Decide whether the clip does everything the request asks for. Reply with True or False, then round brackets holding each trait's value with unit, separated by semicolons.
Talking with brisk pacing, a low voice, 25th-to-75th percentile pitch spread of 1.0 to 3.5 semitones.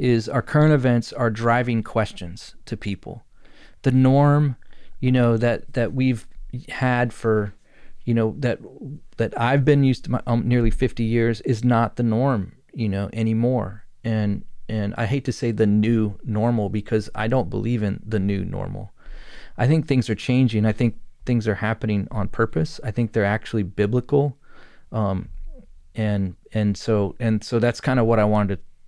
False (175 wpm; 115 Hz; 2.8 semitones)